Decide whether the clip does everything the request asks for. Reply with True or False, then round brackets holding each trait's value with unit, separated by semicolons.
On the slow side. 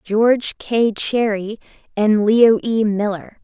True (120 wpm)